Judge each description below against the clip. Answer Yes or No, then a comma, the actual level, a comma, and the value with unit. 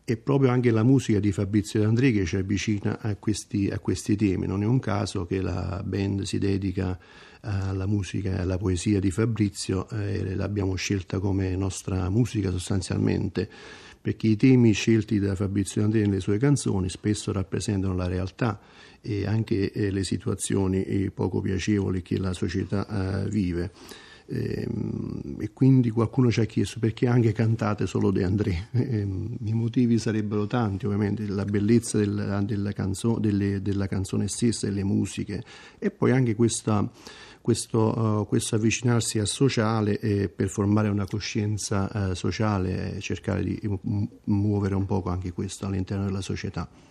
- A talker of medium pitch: No, low, 105 Hz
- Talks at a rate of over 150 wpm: Yes, average, 160 wpm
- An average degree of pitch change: No, narrow, 2.3 semitones